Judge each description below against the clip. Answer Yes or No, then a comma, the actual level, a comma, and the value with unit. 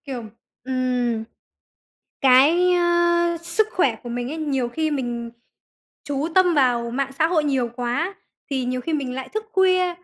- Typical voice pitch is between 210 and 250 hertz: No, very high, 275 Hz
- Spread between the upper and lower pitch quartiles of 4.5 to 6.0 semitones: Yes, wide, 5.5 semitones